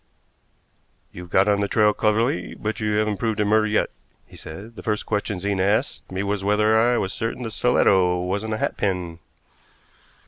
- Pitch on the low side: Yes, low, 105 Hz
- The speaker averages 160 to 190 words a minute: Yes, average, 180 wpm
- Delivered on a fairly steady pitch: Yes, narrow, 2.2 semitones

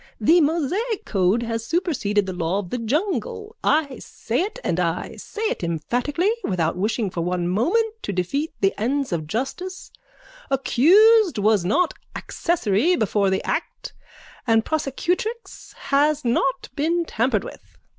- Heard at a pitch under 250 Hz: No, very high, 260 Hz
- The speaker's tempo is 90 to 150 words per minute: Yes, average, 145 wpm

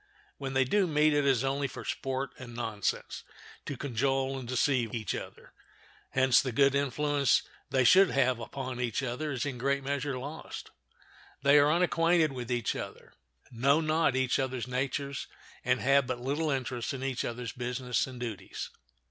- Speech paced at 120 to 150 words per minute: No, average, 175 wpm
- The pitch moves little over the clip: Yes, narrow, 2.3 semitones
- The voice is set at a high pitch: No, low, 135 Hz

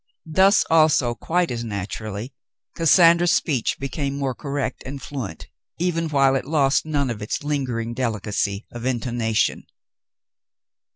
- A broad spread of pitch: No, average, 4.9 semitones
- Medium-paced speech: No, slow, 125 wpm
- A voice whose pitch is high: No, low, 135 Hz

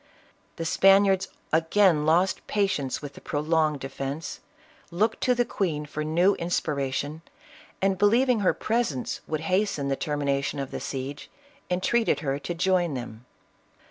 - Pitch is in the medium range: Yes, medium, 160 Hz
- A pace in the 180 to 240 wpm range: No, average, 145 wpm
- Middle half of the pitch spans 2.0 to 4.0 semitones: No, average, 5.1 semitones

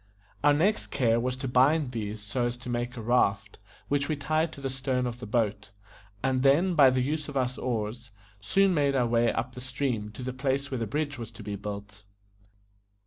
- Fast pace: Yes, fast, 215 wpm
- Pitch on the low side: Yes, low, 125 Hz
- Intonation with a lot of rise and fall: No, average, 3.3 semitones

